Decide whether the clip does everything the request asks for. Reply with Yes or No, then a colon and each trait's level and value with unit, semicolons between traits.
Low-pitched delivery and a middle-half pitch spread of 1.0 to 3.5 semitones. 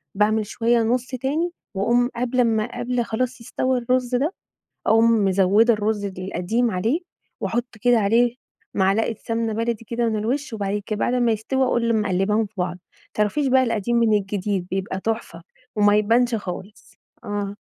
No: high, 225 Hz; average, 2.9 semitones